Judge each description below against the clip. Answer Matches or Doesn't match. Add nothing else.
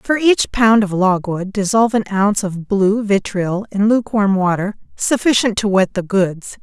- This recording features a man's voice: Doesn't match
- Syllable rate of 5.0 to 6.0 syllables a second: Doesn't match